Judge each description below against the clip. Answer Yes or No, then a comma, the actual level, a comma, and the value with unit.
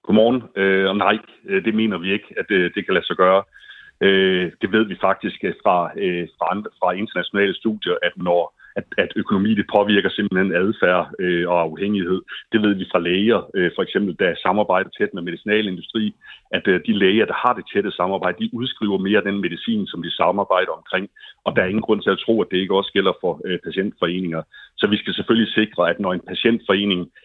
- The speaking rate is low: No, average, 185 wpm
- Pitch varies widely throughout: No, average, 2.8 semitones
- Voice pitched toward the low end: Yes, low, 100 Hz